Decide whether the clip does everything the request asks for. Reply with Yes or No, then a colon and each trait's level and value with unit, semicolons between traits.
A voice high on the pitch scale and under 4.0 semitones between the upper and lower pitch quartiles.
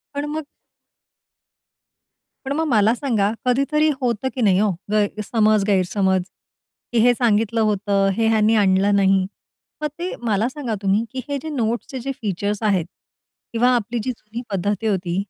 Yes: high, 215 Hz; average, 3.6 semitones